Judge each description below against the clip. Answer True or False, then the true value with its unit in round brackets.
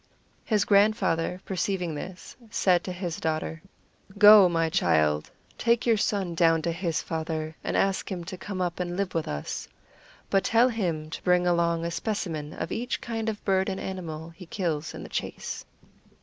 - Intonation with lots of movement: False (3.3 semitones)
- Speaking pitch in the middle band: True (180 Hz)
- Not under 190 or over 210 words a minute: False (175 wpm)